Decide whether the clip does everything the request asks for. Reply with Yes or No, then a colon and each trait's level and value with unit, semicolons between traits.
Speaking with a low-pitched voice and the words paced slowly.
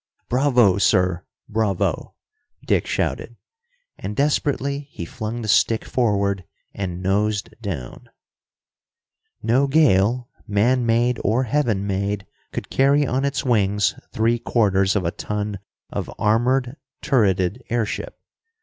Yes: low, 110 Hz; slow, 115 wpm